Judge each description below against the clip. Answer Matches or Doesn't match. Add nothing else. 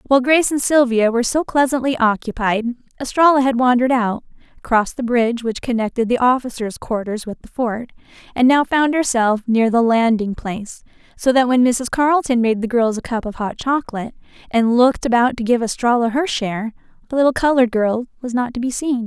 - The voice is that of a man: Doesn't match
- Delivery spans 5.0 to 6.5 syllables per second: Matches